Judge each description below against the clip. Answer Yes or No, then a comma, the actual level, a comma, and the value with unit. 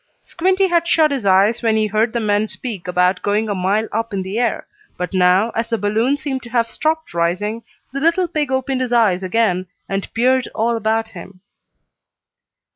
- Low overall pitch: No, high, 225 Hz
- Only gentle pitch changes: No, average, 4.6 semitones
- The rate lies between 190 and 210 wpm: Yes, average, 195 wpm